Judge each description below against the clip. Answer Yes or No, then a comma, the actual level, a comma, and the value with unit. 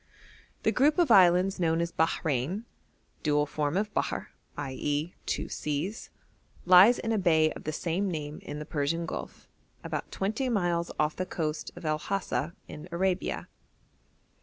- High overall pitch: No, medium, 170 Hz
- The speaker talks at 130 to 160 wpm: Yes, average, 155 wpm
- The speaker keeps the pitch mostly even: No, average, 4.0 semitones